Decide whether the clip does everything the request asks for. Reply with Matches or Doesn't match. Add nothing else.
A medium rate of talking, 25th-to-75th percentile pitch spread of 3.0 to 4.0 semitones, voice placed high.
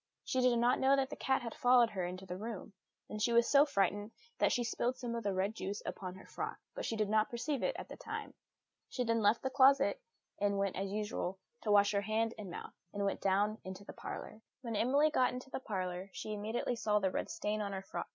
Doesn't match